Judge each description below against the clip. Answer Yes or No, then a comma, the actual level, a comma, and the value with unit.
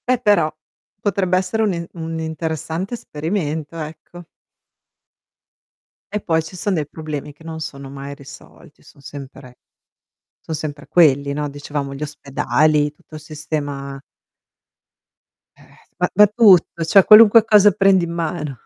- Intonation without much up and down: No, average, 3.9 semitones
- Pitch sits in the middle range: Yes, medium, 160 Hz